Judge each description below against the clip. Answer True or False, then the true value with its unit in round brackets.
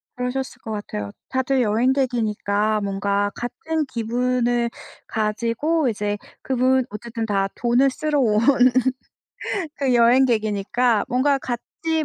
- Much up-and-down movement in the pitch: False (3.6 semitones)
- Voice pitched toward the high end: True (240 Hz)